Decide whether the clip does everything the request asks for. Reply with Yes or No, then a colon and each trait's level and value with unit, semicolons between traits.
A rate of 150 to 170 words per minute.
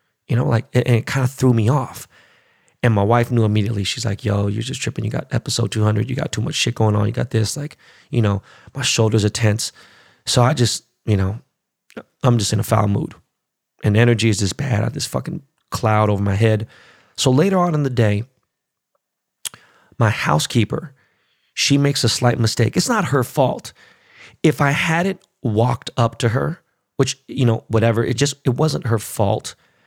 No: fast, 205 wpm